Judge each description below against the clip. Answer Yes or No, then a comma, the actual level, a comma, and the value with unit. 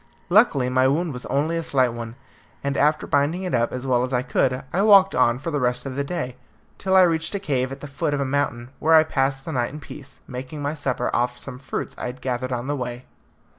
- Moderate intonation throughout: Yes, average, 3.4 semitones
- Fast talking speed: Yes, fast, 250 wpm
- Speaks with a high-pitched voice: No, low, 135 Hz